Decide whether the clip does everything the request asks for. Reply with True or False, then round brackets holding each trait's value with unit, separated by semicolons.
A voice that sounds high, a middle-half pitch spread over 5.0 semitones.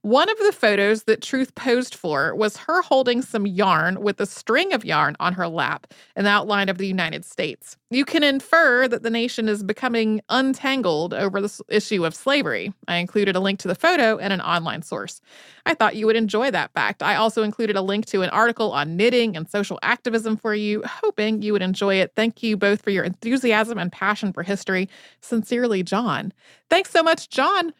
False (215 Hz; 3.5 semitones)